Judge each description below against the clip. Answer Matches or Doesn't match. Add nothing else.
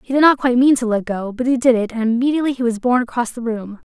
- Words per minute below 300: Doesn't match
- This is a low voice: Doesn't match